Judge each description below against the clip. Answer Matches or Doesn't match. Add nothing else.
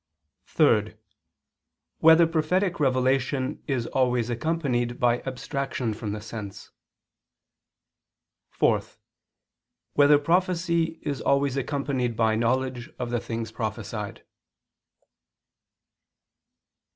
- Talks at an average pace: Doesn't match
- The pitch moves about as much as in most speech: Matches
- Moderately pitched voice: Doesn't match